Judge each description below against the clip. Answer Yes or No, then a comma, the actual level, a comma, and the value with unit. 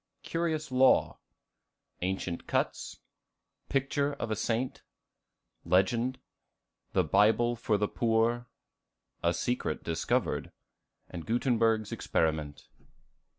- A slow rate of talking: Yes, slow, 85 wpm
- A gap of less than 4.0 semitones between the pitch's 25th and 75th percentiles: No, average, 5.0 semitones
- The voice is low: Yes, low, 115 Hz